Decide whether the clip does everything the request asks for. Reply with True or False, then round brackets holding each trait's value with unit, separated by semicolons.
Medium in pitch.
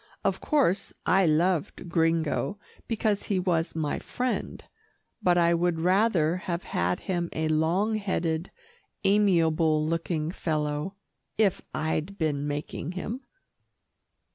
True (170 Hz)